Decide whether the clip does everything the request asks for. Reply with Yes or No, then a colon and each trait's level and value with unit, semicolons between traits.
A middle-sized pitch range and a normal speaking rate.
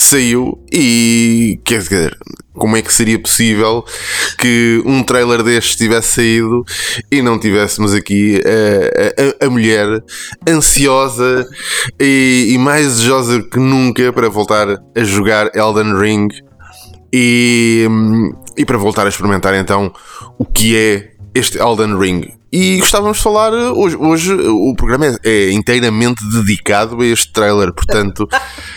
Yes: average, 3.1 semitones; average, 135 wpm